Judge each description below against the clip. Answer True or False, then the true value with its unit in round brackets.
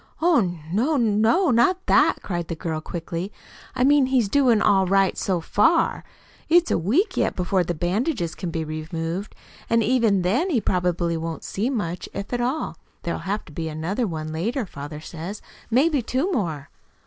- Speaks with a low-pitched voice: False (195 Hz)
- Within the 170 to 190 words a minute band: True (175 wpm)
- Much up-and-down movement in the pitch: True (6.9 semitones)